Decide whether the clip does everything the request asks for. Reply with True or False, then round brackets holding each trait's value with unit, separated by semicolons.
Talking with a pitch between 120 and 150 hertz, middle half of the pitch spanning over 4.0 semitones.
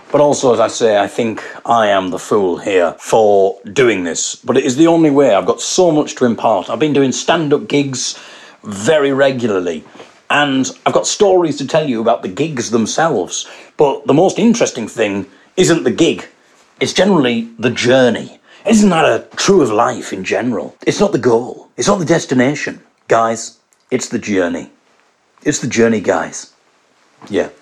True (140 Hz; 5.0 semitones)